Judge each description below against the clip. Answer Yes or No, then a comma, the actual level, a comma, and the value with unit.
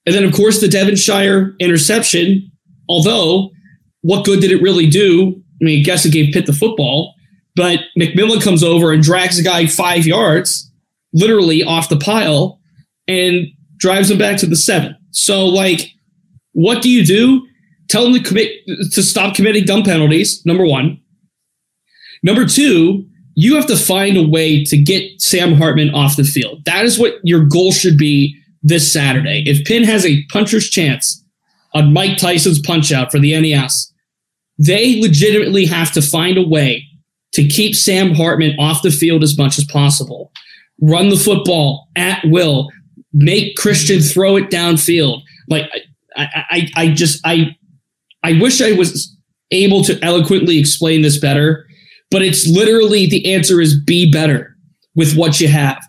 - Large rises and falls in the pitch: No, average, 3.7 semitones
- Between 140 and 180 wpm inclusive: Yes, average, 165 wpm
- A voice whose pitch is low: No, medium, 170 Hz